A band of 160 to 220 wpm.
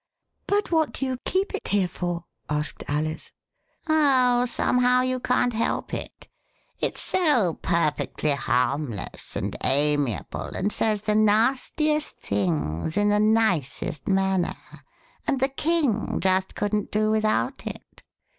No: slow, 135 wpm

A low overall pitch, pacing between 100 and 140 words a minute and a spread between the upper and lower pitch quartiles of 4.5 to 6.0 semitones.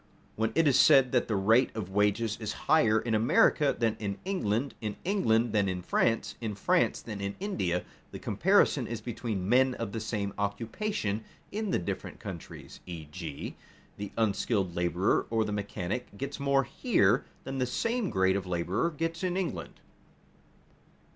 No: low, 110 Hz; average, 165 wpm; average, 4.9 semitones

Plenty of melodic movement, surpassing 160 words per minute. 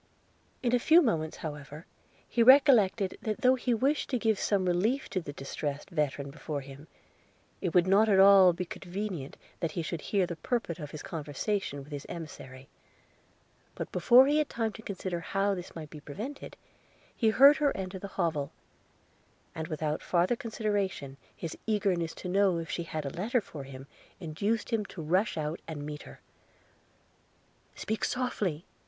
Yes: wide, 5.9 semitones; average, 170 wpm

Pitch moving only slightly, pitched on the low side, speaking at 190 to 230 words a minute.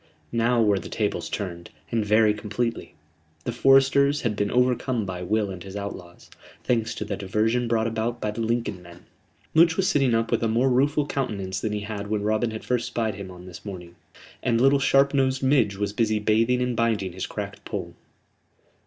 No: average, 3.4 semitones; low, 110 Hz; average, 195 wpm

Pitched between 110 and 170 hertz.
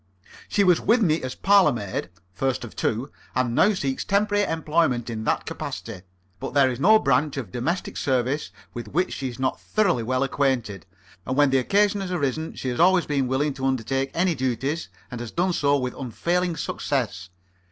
Yes: low, 135 Hz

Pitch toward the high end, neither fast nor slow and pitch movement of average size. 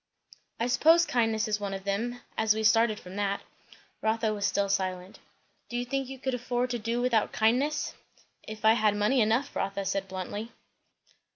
Yes: high, 220 Hz; average, 180 wpm; average, 3.3 semitones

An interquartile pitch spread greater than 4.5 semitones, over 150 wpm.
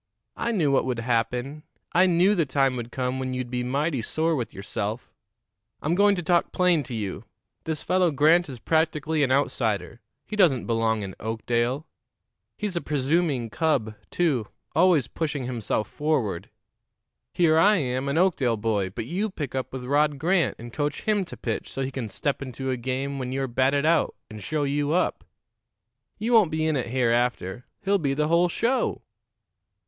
Yes: average, 5.0 semitones; average, 180 wpm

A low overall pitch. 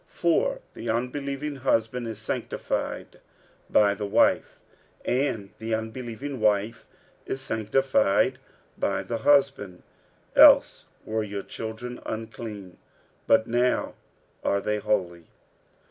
Yes: low, 110 Hz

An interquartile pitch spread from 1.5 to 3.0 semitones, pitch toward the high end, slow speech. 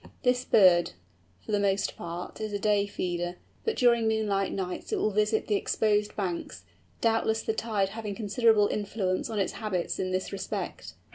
No: narrow, 2.6 semitones; high, 205 Hz; average, 170 wpm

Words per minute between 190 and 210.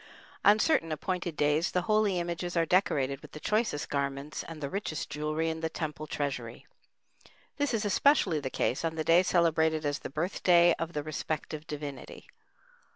No: average, 170 wpm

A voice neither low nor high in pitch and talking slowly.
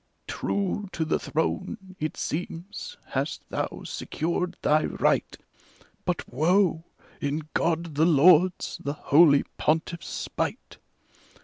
Yes: medium, 165 Hz; slow, 110 wpm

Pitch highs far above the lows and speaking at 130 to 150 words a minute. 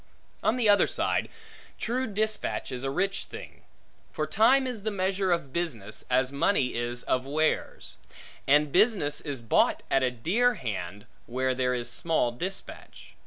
No: wide, 8.0 semitones; average, 160 wpm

